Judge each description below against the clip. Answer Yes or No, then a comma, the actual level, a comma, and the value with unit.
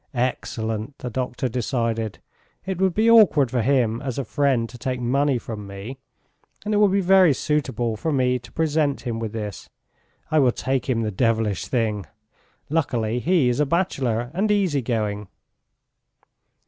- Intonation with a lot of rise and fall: No, average, 4.7 semitones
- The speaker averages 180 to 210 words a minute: No, average, 165 wpm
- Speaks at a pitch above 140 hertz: No, low, 125 Hz